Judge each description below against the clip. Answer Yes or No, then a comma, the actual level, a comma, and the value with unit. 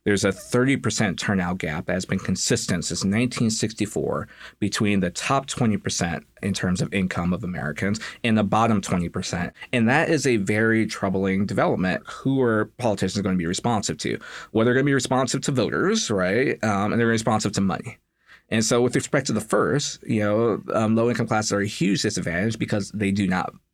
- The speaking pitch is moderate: No, low, 110 Hz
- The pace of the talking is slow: No, average, 195 wpm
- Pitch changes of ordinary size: Yes, average, 3.6 semitones